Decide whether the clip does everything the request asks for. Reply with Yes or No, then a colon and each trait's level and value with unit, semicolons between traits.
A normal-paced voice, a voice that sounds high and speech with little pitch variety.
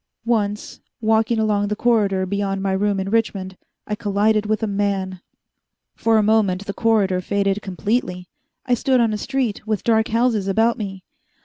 Yes: average, 170 wpm; high, 210 Hz; narrow, 2.3 semitones